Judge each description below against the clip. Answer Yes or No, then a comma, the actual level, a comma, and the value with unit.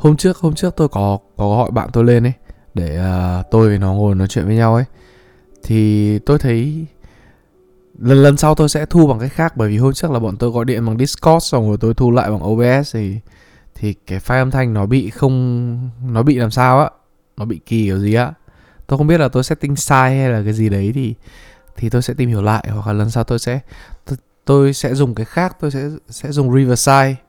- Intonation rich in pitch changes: No, average, 4.2 semitones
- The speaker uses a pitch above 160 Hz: No, low, 125 Hz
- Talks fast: No, average, 235 wpm